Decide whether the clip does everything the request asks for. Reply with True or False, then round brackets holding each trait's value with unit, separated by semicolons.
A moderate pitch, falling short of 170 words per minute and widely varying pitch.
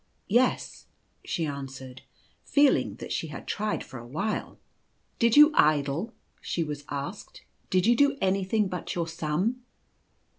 True (180 Hz; 160 wpm; 7.7 semitones)